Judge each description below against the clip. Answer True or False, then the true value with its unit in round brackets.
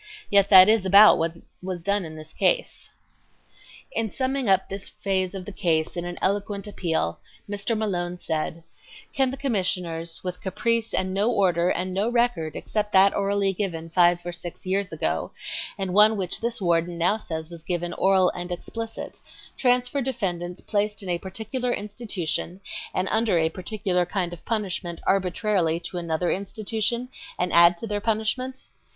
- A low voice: False (190 Hz)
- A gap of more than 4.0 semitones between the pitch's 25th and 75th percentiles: False (3.5 semitones)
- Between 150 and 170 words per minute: True (165 wpm)